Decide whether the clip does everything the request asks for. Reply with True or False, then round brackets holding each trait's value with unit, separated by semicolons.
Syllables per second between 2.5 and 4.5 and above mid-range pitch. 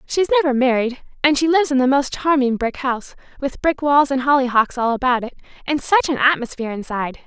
False (6.2 syllables/s; 270 Hz)